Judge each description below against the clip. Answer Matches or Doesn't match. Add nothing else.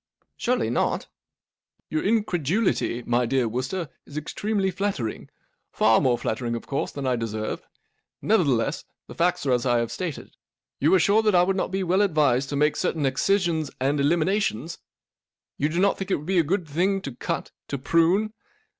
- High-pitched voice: Doesn't match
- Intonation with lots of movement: Matches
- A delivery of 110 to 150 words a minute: Doesn't match